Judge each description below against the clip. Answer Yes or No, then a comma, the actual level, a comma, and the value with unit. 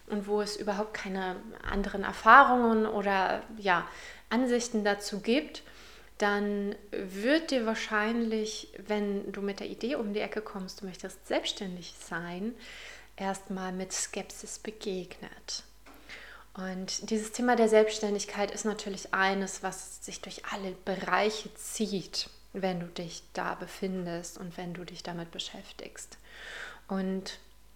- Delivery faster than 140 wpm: No, average, 130 wpm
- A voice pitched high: Yes, high, 205 Hz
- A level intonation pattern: Yes, narrow, 2.3 semitones